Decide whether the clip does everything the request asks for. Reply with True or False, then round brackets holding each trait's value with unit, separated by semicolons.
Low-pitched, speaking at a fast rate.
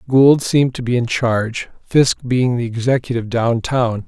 False (120 Hz; 175 wpm)